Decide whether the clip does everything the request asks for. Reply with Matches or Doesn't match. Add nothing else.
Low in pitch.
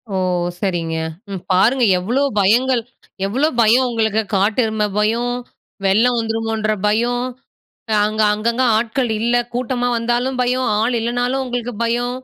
Doesn't match